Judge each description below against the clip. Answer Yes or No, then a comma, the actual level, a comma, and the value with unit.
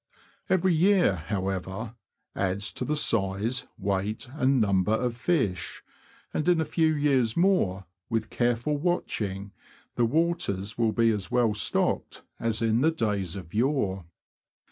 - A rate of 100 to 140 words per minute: Yes, slow, 135 wpm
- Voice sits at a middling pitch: No, low, 115 Hz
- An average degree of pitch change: No, wide, 6.7 semitones